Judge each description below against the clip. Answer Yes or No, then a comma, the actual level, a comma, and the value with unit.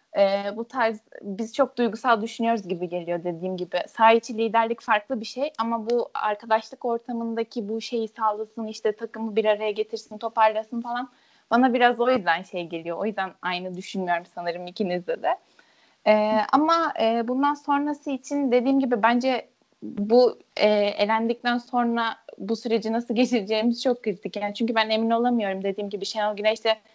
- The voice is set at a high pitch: Yes, high, 225 Hz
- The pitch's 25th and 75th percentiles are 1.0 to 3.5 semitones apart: Yes, narrow, 2.4 semitones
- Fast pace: Yes, fast, 160 wpm